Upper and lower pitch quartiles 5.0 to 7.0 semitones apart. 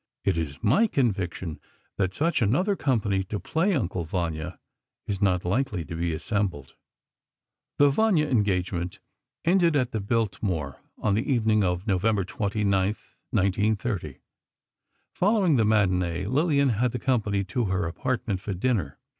Yes: wide, 5.6 semitones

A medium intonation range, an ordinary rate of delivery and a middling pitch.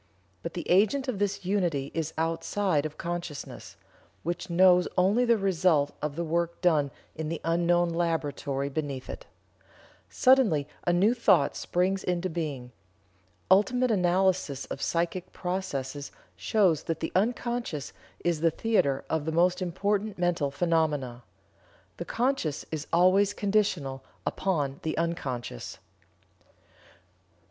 No: average, 4.1 semitones; slow, 125 wpm; medium, 170 Hz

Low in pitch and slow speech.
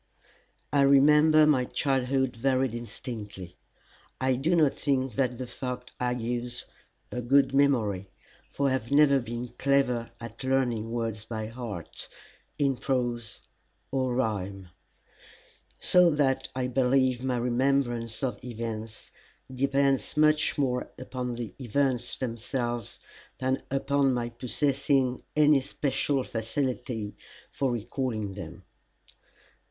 Yes: low, 125 Hz; slow, 115 wpm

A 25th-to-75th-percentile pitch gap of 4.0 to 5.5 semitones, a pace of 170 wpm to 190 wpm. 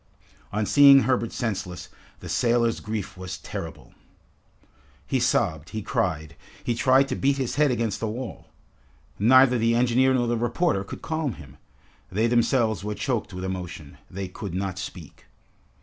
No: average, 4.7 semitones; average, 155 wpm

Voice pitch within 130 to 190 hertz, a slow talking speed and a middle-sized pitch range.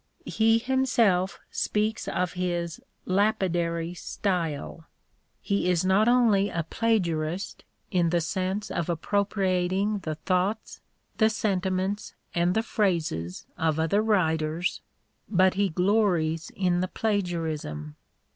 Yes: medium, 185 Hz; slow, 120 wpm; average, 3.5 semitones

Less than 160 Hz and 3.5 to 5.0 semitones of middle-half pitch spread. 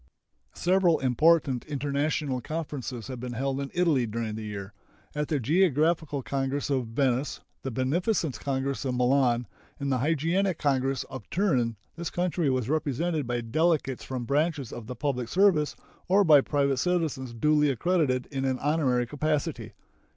Yes: medium, 140 Hz; average, 3.8 semitones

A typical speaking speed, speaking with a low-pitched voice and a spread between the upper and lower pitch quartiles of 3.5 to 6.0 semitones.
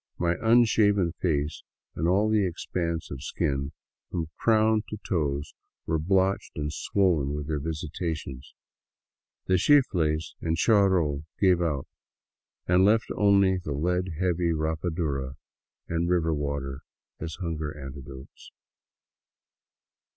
No: slow, 115 wpm; very low, 85 Hz; average, 4.0 semitones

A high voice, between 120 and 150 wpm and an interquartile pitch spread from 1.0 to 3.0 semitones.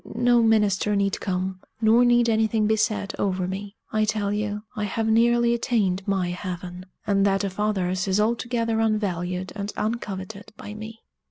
No: high, 210 Hz; average, 165 wpm; average, 2.7 semitones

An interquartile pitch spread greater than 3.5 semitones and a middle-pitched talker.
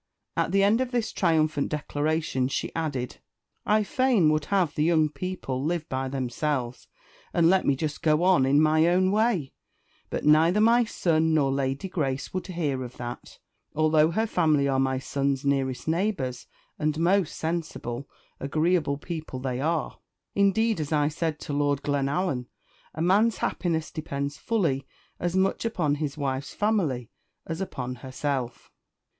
Yes: average, 4.5 semitones; medium, 155 Hz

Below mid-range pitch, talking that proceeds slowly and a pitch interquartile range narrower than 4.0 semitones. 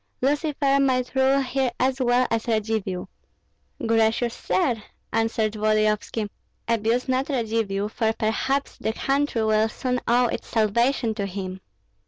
No: high, 230 Hz; slow, 130 wpm; average, 3.2 semitones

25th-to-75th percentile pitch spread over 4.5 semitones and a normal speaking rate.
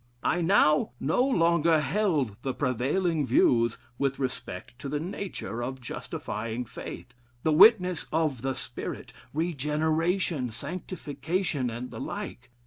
No: average, 5.0 semitones; slow, 125 wpm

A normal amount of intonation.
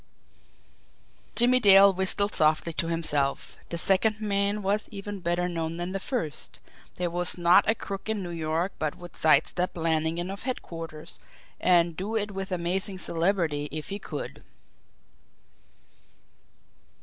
Yes: average, 3.3 semitones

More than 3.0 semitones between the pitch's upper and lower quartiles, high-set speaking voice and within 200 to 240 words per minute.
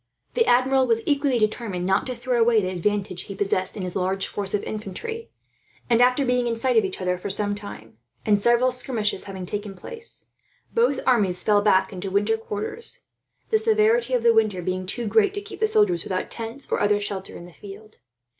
Yes: average, 4.8 semitones; high, 215 Hz; fast, 205 wpm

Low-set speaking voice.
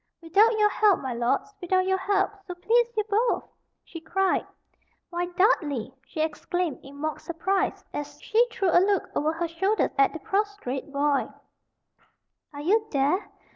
No: very high, 360 Hz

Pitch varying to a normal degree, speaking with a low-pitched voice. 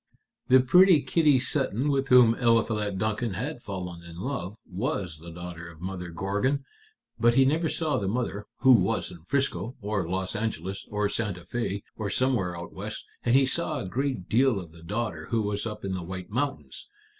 No: wide, 5.8 semitones; low, 105 Hz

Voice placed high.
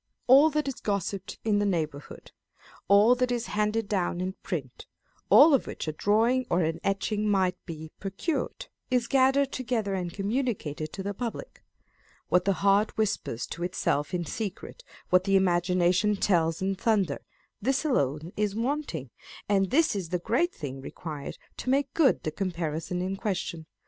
Yes: high, 195 Hz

